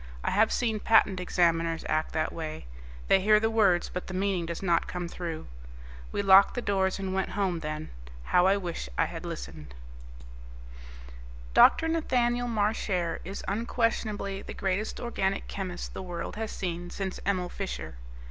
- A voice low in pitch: No, high, 190 Hz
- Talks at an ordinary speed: Yes, average, 160 wpm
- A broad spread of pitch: No, average, 3.2 semitones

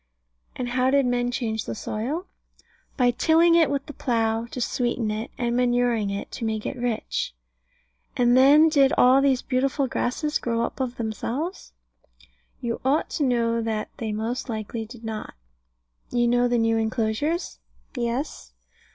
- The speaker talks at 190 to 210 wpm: No, average, 160 wpm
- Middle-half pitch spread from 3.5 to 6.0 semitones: No, average, 2.8 semitones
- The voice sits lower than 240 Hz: No, high, 245 Hz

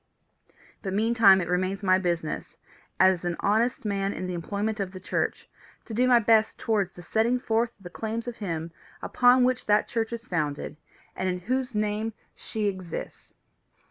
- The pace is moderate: Yes, average, 175 wpm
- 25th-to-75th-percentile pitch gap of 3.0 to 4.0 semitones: Yes, average, 3.5 semitones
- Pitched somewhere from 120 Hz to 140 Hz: No, high, 205 Hz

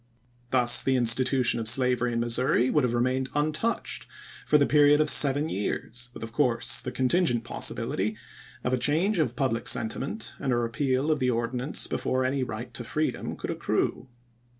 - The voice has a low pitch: Yes, low, 130 Hz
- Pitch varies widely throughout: No, average, 3.3 semitones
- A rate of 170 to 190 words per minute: Yes, average, 175 wpm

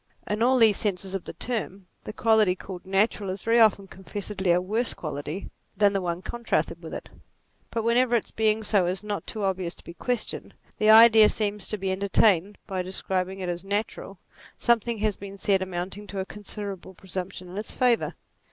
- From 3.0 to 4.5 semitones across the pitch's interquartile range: No, narrow, 2.6 semitones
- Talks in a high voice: Yes, high, 200 Hz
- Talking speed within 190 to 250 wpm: Yes, average, 200 wpm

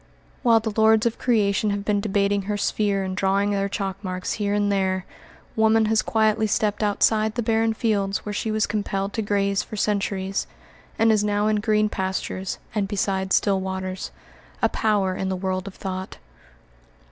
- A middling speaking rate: Yes, average, 180 wpm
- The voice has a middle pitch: No, high, 205 Hz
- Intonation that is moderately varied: No, narrow, 1.8 semitones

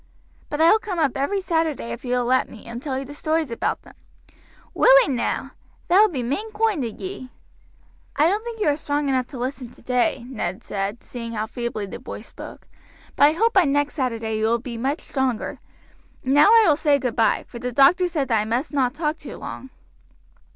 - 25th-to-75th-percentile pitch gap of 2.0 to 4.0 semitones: No, average, 5.1 semitones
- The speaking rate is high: Yes, fast, 220 wpm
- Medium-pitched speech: No, very high, 275 Hz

